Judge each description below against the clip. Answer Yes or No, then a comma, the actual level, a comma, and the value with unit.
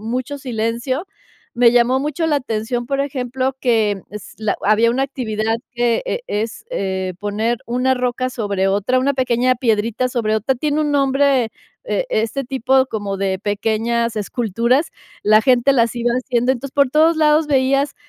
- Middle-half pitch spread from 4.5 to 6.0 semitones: No, average, 3.4 semitones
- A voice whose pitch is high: Yes, high, 245 Hz